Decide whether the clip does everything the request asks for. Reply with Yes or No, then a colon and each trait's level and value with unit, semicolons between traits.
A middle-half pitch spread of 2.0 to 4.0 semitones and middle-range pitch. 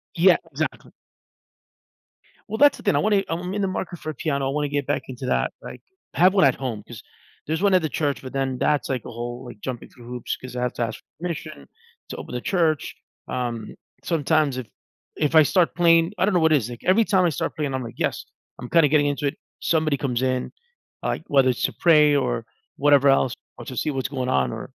No: average, 4.6 semitones; medium, 145 Hz